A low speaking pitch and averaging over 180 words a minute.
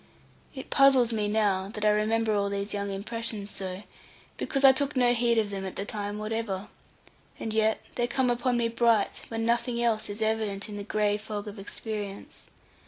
No: high, 215 Hz; average, 190 wpm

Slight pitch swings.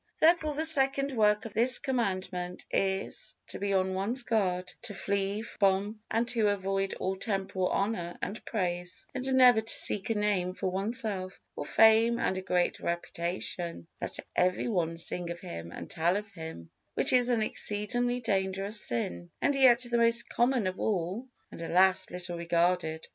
No: average, 4.2 semitones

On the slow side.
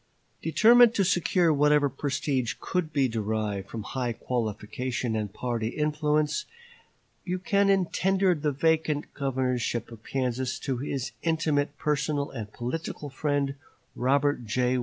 Yes: slow, 120 wpm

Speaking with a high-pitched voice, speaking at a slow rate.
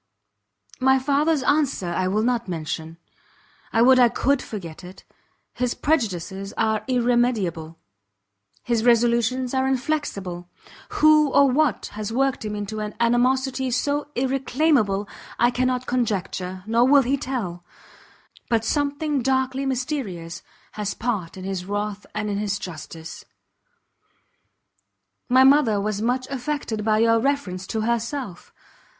Yes: high, 235 Hz; slow, 125 wpm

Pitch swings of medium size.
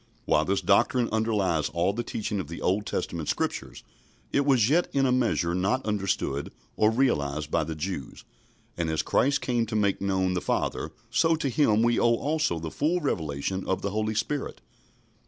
No: wide, 6.4 semitones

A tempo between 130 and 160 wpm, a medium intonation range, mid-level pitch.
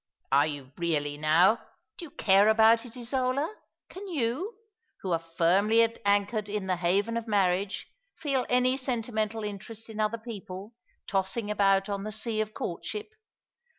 No: average, 150 wpm; average, 3.4 semitones; high, 215 Hz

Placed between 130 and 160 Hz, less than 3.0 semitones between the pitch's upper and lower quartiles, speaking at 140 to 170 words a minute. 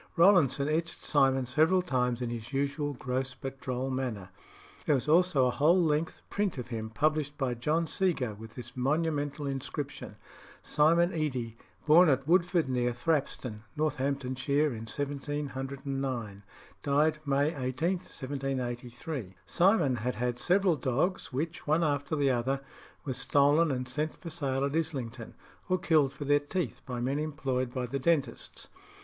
No: medium, 140 Hz; average, 3.6 semitones; average, 150 wpm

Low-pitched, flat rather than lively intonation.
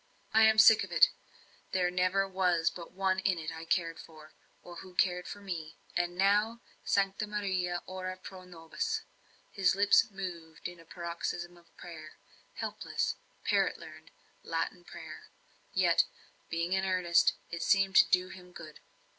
No: medium, 180 Hz; narrow, 2.2 semitones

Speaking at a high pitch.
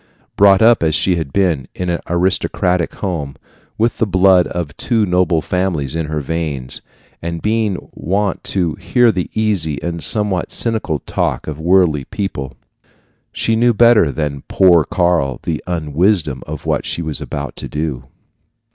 No: very low, 85 Hz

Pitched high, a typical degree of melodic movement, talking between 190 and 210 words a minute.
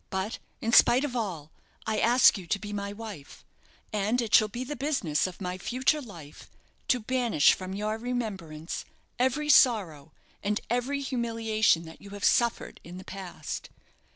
No: high, 215 Hz; average, 4.8 semitones; average, 165 wpm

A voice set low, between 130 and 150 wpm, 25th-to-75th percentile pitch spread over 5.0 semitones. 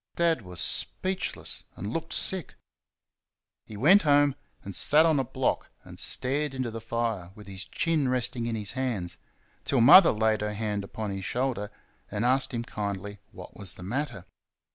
No: low, 115 Hz; average, 170 wpm; wide, 5.4 semitones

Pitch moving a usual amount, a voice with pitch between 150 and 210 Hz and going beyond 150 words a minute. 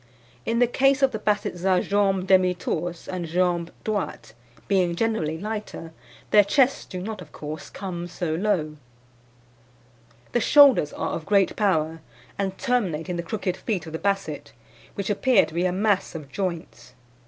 Yes: average, 3.8 semitones; medium, 185 Hz; average, 165 wpm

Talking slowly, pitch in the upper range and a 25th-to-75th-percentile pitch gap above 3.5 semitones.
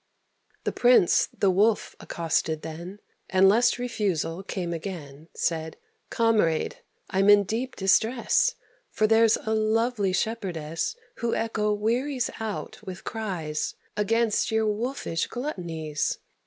Yes: slow, 115 wpm; high, 205 Hz; average, 4.8 semitones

